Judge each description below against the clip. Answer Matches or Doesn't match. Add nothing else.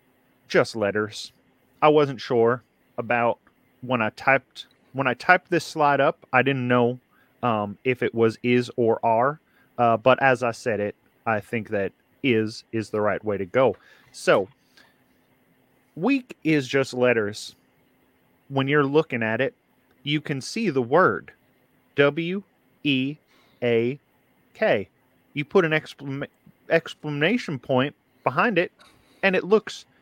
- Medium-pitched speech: Doesn't match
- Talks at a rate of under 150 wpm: Matches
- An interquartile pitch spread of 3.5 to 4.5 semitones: Matches